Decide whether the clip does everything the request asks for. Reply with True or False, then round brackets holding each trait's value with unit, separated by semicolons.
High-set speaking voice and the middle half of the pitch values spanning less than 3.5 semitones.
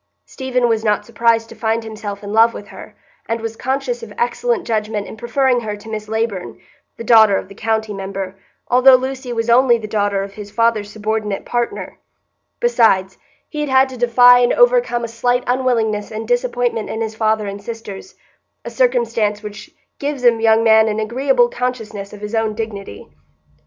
True (225 Hz; 2.7 semitones)